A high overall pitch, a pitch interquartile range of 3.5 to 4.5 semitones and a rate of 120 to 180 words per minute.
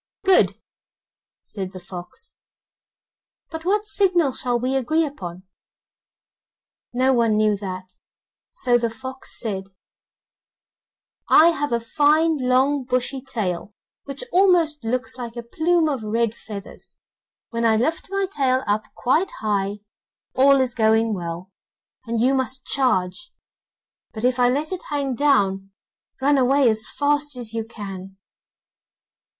No: very high, 250 Hz; average, 4.9 semitones; slow, 135 wpm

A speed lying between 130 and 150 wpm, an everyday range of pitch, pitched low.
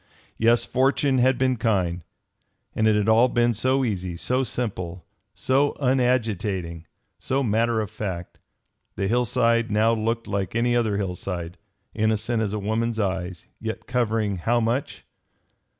Yes: average, 140 wpm; average, 3.4 semitones; low, 110 Hz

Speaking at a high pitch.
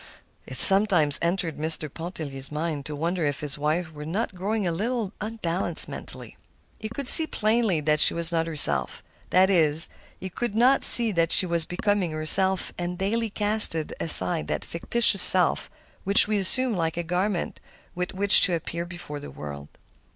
No: medium, 175 Hz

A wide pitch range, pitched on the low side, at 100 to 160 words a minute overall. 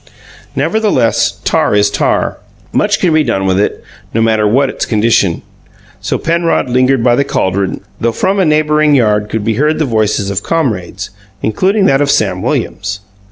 No: wide, 6.6 semitones; low, 120 Hz; average, 170 wpm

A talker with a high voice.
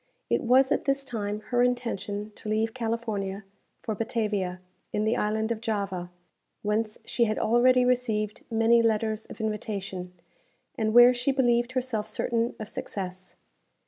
Yes: high, 220 Hz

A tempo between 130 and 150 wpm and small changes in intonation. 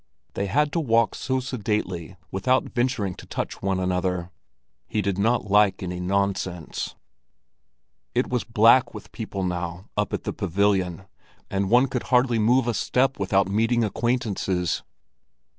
No: average, 145 wpm; average, 4.5 semitones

